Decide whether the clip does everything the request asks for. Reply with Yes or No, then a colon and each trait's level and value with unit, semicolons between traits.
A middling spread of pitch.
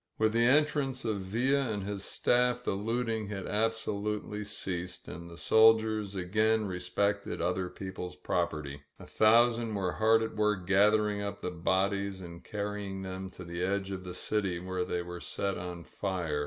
Yes: average, 3.2 semitones